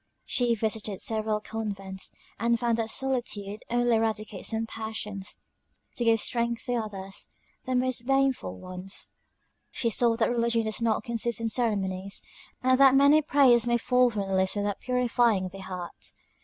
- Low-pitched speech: No, high, 225 Hz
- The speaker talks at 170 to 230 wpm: No, average, 155 wpm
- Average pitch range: Yes, average, 3.0 semitones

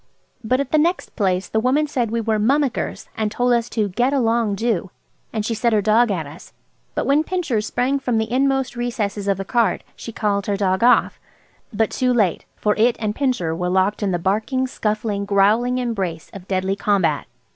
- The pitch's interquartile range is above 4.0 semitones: No, average, 3.7 semitones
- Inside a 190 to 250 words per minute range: Yes, average, 200 wpm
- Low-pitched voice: No, high, 220 Hz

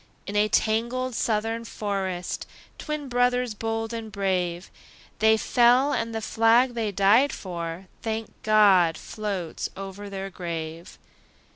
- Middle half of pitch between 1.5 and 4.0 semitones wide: Yes, average, 3.2 semitones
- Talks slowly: Yes, slow, 125 wpm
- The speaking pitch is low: No, high, 215 Hz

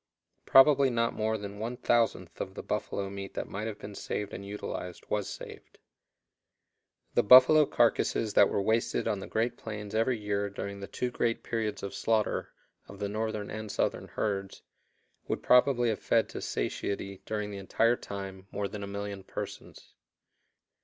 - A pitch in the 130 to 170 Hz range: No, low, 105 Hz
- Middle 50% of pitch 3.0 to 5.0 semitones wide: No, narrow, 2.4 semitones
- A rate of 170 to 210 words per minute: Yes, average, 175 wpm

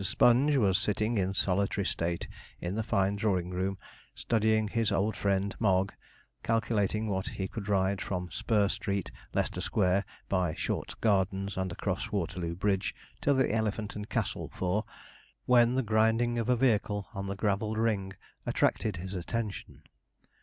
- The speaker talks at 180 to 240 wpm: No, average, 155 wpm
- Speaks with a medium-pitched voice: No, low, 100 Hz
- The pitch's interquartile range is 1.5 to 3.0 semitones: Yes, narrow, 2.6 semitones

